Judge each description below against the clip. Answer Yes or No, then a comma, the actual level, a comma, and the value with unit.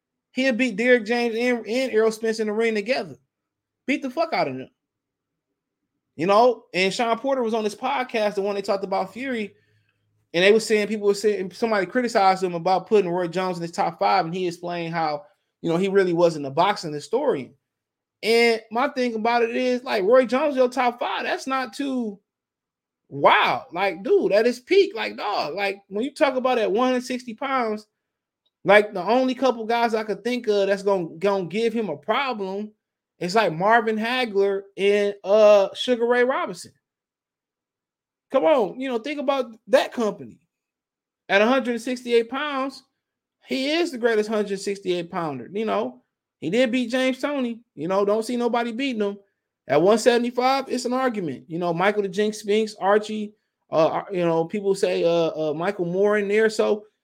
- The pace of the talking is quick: No, average, 185 wpm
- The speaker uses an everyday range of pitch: Yes, average, 4.1 semitones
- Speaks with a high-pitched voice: Yes, high, 220 Hz